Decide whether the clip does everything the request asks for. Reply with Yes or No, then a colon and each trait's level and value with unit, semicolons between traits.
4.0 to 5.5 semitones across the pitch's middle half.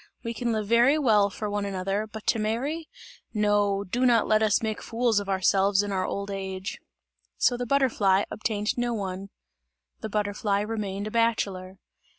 No: narrow, 2.5 semitones